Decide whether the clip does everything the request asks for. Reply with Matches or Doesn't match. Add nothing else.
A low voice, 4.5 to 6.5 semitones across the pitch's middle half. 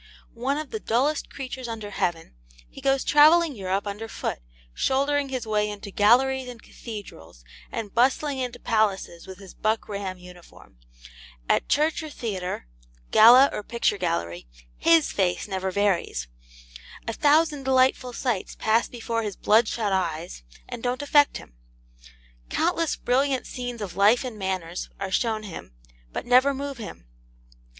Doesn't match